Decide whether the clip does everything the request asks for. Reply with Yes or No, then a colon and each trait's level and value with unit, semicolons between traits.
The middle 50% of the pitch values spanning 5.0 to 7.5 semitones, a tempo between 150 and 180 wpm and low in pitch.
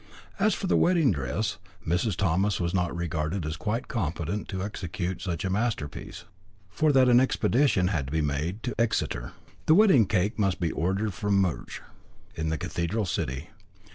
Yes: average, 5.3 semitones; average, 170 wpm; very low, 95 Hz